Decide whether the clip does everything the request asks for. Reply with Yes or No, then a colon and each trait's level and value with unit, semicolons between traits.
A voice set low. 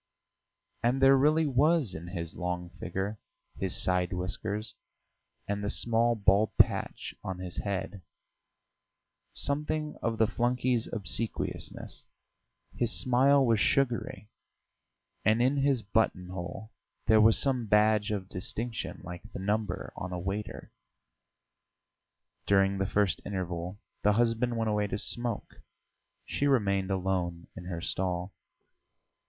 Yes: low, 105 Hz